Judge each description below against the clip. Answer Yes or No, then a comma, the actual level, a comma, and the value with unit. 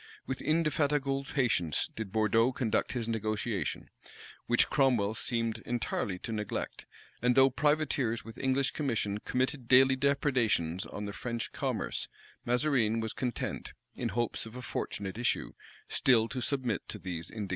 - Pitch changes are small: No, average, 3.5 semitones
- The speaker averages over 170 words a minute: No, average, 145 wpm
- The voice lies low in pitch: Yes, low, 120 Hz